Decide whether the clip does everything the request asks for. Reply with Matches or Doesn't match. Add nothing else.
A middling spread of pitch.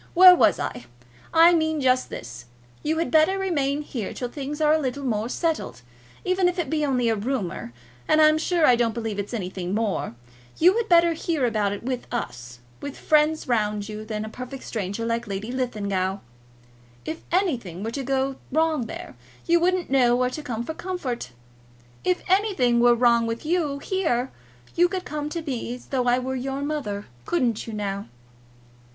Doesn't match